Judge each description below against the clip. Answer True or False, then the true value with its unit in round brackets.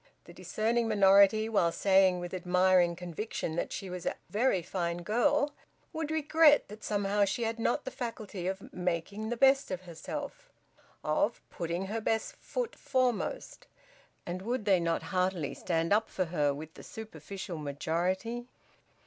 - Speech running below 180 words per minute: True (155 wpm)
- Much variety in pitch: False (4.5 semitones)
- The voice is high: True (195 Hz)